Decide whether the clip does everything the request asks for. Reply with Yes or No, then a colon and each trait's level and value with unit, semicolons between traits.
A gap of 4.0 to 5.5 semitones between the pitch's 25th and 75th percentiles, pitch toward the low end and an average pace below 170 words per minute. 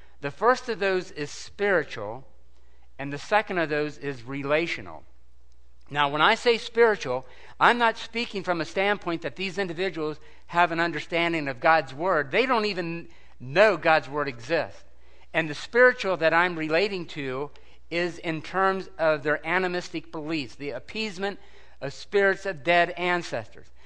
No: average, 5.0 semitones; medium, 165 Hz; average, 155 wpm